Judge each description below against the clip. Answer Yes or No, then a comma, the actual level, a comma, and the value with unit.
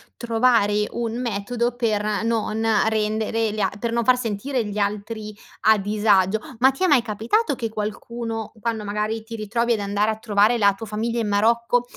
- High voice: Yes, high, 220 Hz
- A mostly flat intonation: Yes, narrow, 2.0 semitones